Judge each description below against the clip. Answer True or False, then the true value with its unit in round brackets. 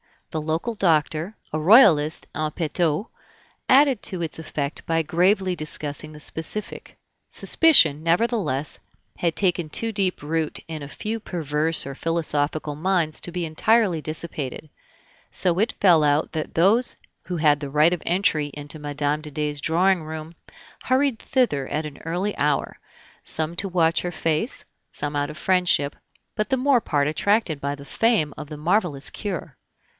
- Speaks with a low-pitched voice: False (160 Hz)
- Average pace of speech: True (160 wpm)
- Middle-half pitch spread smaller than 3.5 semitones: False (4.0 semitones)